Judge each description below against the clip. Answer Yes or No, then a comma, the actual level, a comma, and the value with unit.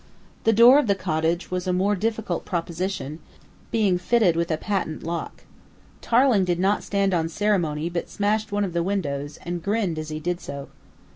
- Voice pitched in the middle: Yes, medium, 180 Hz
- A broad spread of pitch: No, average, 3.7 semitones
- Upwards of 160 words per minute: Yes, average, 185 wpm